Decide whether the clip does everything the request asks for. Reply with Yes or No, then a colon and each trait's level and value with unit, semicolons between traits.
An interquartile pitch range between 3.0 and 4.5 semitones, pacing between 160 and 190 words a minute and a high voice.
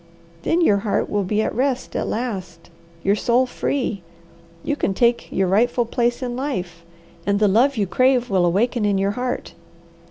Yes: average, 4.2 semitones; average, 180 wpm; high, 225 Hz